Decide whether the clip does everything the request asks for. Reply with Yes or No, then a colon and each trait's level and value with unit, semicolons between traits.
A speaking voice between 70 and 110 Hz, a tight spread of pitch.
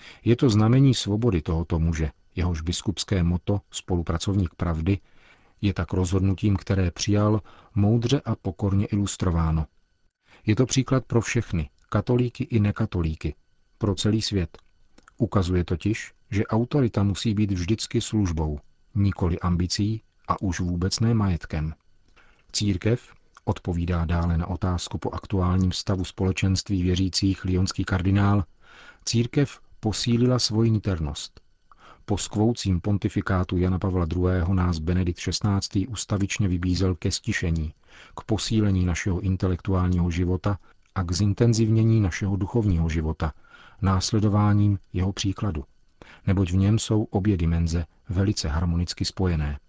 No: very low, 95 Hz; average, 3.2 semitones